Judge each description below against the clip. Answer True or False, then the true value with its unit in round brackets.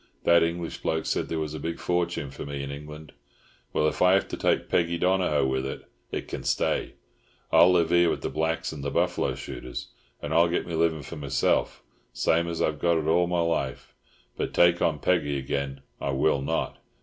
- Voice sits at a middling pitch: False (80 Hz)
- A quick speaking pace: True (210 wpm)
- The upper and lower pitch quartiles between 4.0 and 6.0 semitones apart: False (3.2 semitones)